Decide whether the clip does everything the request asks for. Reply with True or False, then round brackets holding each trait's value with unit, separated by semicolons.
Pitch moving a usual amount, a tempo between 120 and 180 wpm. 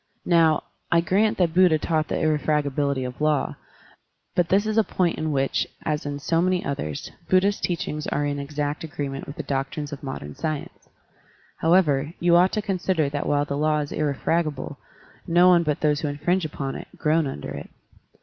False (3.2 semitones; 190 wpm)